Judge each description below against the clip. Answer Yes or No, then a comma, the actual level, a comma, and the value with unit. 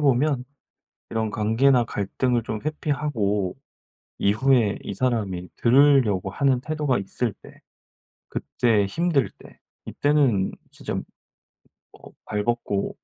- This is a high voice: No, low, 120 Hz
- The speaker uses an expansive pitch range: No, average, 5.0 semitones